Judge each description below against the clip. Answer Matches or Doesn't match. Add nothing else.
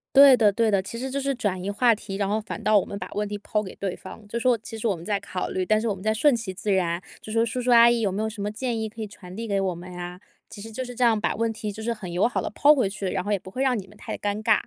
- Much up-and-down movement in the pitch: Doesn't match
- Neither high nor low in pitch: Doesn't match